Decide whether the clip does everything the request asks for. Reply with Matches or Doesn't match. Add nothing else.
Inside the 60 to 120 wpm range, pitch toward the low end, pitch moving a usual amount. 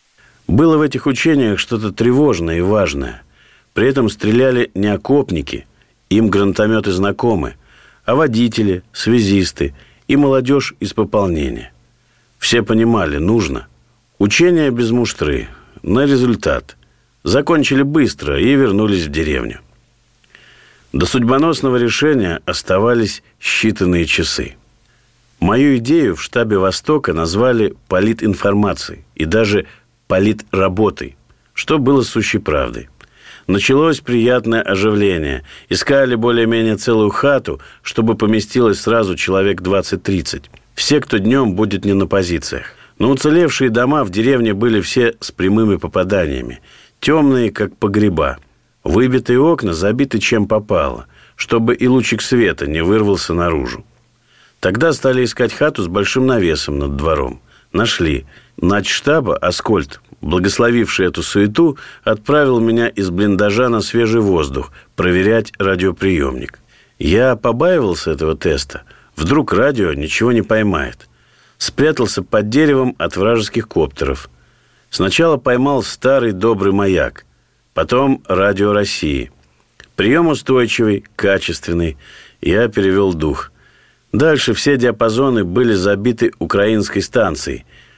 Matches